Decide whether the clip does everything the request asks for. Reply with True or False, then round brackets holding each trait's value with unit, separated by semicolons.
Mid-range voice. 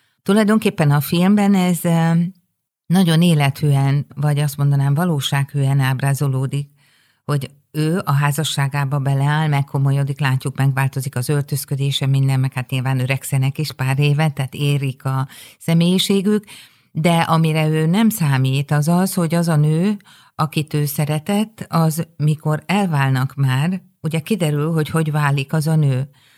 True (145 Hz)